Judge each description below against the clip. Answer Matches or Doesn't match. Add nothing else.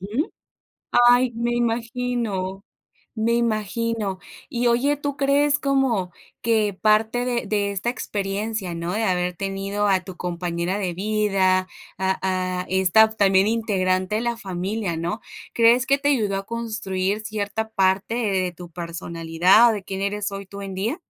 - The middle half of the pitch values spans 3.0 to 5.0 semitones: Matches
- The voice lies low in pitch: Doesn't match